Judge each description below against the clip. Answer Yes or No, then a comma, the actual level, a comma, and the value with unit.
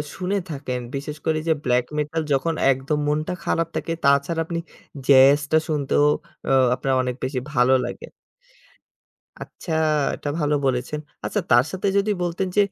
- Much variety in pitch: No, average, 3.6 semitones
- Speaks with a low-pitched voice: No, medium, 150 Hz